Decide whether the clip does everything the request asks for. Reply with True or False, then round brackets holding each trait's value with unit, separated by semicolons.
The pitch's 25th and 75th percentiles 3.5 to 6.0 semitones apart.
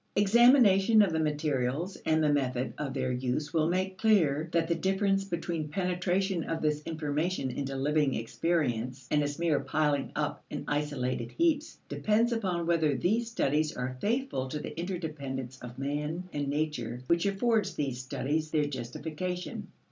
True (5.0 semitones)